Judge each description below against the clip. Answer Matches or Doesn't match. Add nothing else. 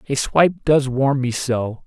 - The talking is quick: Doesn't match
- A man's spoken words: Matches